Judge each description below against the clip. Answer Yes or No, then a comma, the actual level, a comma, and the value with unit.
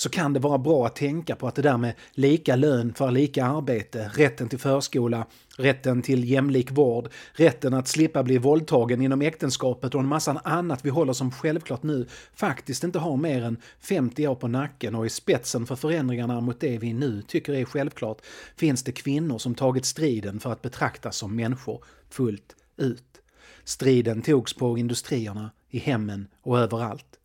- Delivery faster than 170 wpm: Yes, average, 180 wpm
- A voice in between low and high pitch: No, low, 130 Hz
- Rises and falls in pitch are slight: No, average, 3.3 semitones